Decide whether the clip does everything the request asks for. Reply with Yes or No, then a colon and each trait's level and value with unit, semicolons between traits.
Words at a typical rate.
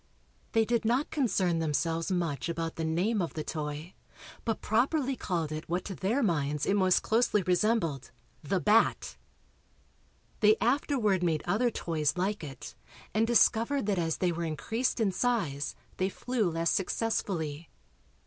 Yes: average, 150 wpm